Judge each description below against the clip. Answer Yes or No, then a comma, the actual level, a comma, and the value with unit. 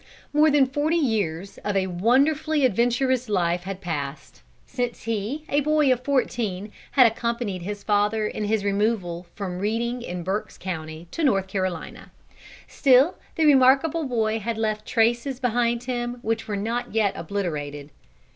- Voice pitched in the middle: No, high, 220 Hz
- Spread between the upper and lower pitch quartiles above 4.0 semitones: Yes, average, 4.8 semitones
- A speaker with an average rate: Yes, average, 150 wpm